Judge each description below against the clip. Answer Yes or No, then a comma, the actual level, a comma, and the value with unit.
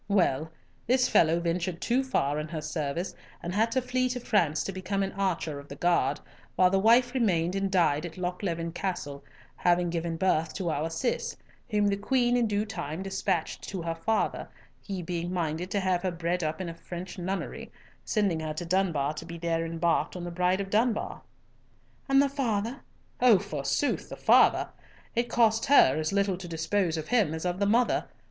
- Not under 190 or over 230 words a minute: Yes, average, 195 wpm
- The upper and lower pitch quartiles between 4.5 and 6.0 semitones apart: No, average, 3.8 semitones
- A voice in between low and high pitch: Yes, medium, 180 Hz